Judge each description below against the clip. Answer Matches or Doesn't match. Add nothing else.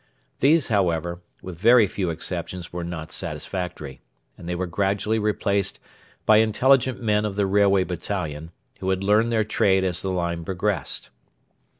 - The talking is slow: Doesn't match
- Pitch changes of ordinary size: Matches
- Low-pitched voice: Matches